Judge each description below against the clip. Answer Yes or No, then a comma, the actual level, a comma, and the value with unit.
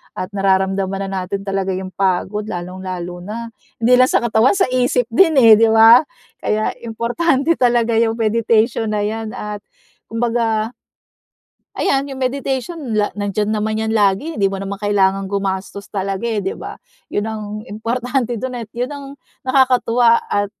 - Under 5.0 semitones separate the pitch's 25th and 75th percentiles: Yes, average, 3.5 semitones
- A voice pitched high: Yes, high, 220 Hz